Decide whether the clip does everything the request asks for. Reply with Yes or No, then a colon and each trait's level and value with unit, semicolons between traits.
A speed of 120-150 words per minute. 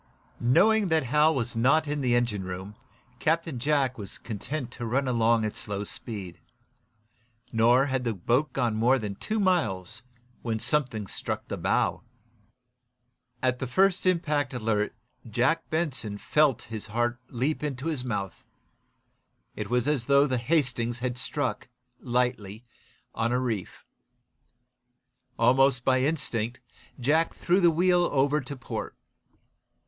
Yes: average, 140 wpm